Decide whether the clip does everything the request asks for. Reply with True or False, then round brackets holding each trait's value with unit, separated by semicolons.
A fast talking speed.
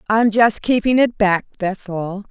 False (180 wpm)